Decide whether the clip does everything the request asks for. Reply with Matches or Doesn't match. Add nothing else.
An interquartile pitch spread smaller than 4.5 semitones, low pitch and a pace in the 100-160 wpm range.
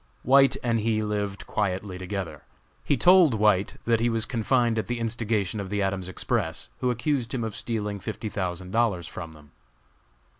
Doesn't match